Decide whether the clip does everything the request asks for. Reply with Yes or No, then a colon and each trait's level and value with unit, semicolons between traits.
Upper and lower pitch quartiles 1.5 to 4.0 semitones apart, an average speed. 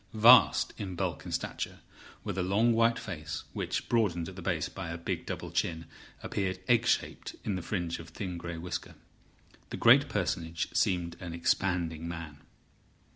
Yes: average, 2.7 semitones; average, 170 wpm